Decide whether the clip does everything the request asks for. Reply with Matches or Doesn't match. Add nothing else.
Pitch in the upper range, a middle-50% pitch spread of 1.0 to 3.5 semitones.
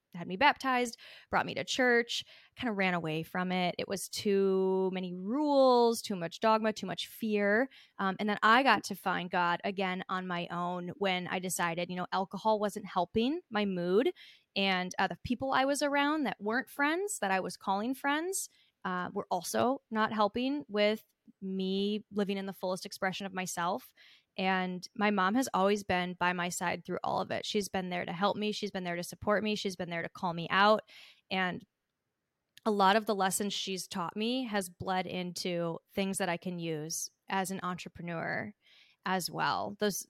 Matches